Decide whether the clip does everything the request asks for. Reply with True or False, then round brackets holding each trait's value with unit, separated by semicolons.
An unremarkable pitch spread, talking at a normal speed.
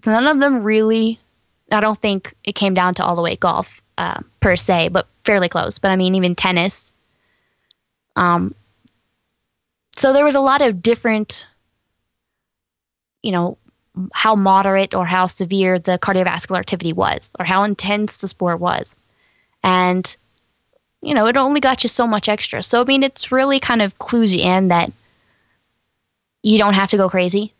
True (3.9 semitones; 170 wpm)